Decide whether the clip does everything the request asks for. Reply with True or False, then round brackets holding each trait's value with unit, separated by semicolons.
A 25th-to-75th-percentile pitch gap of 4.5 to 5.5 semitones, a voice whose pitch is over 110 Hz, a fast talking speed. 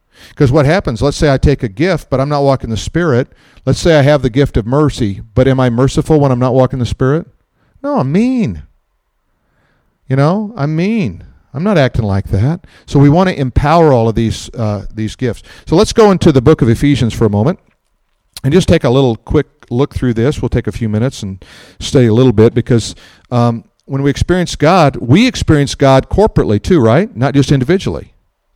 True (4.8 semitones; 135 Hz; 210 wpm)